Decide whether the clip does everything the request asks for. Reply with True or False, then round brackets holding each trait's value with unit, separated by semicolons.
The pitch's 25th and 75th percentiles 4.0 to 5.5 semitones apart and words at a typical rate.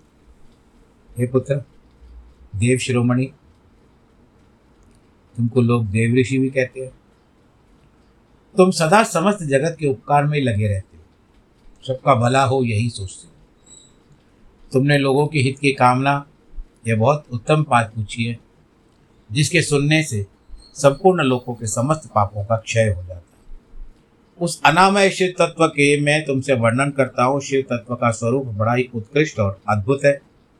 True (4.3 semitones; 140 wpm)